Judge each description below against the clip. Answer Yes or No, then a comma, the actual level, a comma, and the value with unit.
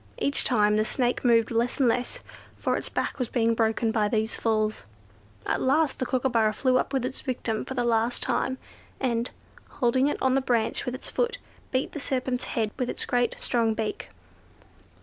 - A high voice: Yes, high, 245 Hz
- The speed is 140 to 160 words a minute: No, average, 190 wpm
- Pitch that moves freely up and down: No, narrow, 2.5 semitones